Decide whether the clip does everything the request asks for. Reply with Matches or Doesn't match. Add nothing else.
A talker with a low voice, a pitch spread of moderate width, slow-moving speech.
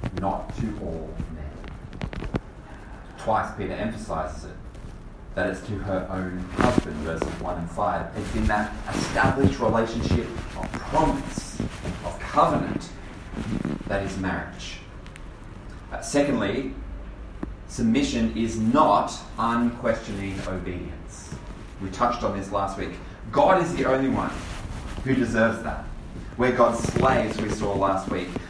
Matches